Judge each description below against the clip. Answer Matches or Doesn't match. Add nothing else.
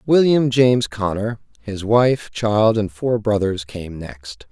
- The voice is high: Doesn't match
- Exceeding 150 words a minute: Doesn't match